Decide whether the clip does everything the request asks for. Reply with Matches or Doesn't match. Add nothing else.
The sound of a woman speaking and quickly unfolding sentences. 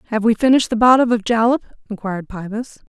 Doesn't match